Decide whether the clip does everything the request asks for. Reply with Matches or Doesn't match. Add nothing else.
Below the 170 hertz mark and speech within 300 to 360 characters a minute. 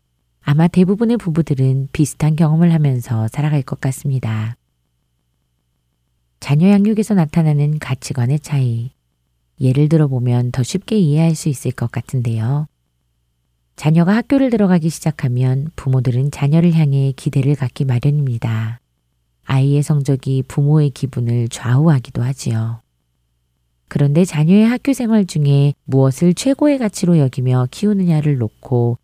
Matches